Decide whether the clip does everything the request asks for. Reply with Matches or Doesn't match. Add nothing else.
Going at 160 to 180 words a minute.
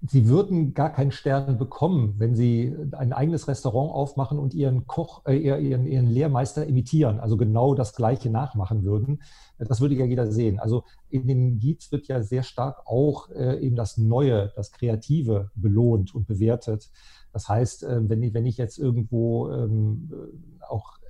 Matches